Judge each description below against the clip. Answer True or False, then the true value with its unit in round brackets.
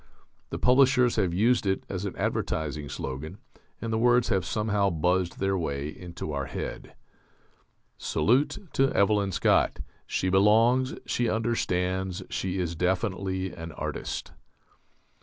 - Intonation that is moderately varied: True (4.2 semitones)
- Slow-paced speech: True (130 wpm)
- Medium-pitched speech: False (95 Hz)